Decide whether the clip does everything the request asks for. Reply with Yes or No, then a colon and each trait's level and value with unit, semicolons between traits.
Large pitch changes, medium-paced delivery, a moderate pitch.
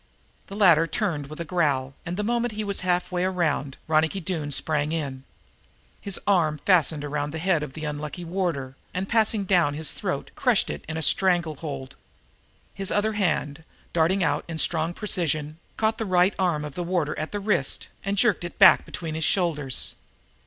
No: average, 4.0 semitones; average, 190 wpm; medium, 165 Hz